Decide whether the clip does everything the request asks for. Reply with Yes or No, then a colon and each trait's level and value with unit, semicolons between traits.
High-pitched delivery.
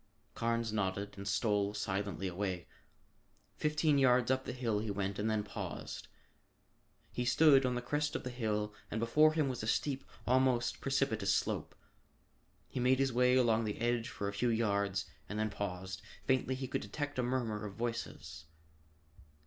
No: low, 115 Hz